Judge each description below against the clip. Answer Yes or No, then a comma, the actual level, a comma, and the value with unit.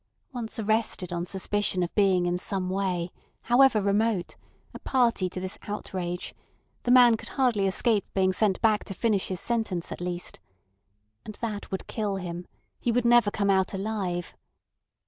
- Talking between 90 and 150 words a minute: No, average, 165 wpm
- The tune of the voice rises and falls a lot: No, average, 3.4 semitones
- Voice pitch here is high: Yes, high, 200 Hz